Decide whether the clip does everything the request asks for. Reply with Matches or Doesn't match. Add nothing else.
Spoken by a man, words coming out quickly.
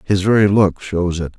Matches